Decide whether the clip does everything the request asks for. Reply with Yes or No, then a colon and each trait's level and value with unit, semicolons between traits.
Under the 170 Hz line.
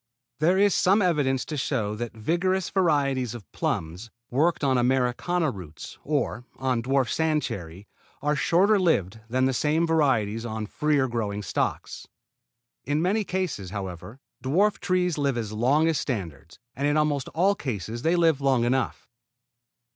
Yes: low, 135 Hz